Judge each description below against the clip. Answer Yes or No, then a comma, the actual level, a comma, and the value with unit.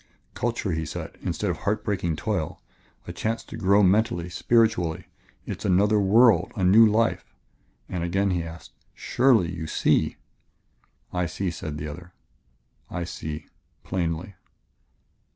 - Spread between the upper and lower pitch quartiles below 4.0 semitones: No, average, 4.3 semitones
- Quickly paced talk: No, average, 145 wpm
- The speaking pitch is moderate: No, very low, 95 Hz